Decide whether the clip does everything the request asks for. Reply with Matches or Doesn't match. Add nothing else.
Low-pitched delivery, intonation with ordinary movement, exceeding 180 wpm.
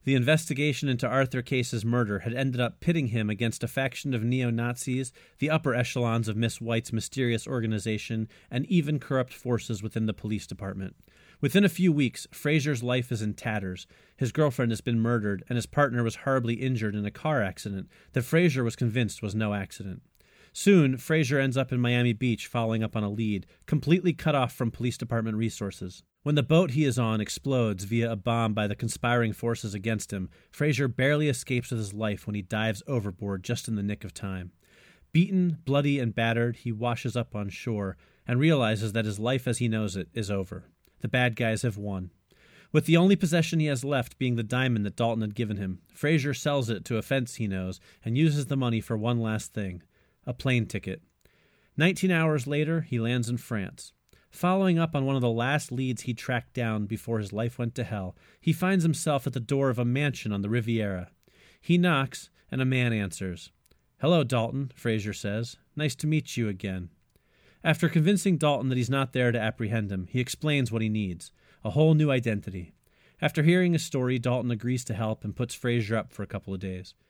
Matches